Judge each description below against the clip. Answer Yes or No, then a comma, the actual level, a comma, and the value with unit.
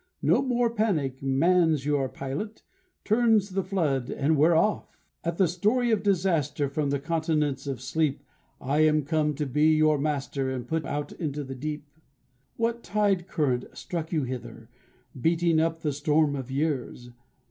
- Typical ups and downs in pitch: Yes, average, 4.1 semitones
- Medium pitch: Yes, medium, 155 Hz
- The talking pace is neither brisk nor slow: Yes, average, 165 wpm